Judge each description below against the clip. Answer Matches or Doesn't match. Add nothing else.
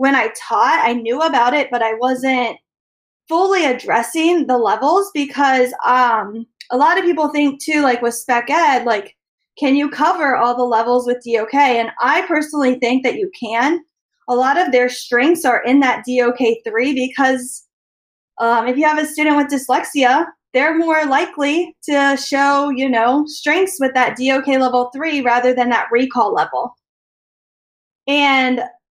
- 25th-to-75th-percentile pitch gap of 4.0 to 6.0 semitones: Doesn't match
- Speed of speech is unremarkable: Matches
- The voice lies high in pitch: Matches